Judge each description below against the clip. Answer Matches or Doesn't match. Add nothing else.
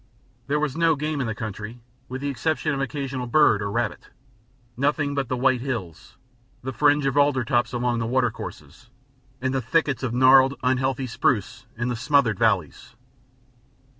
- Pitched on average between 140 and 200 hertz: Doesn't match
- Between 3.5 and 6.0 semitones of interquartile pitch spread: Doesn't match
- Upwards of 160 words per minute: Matches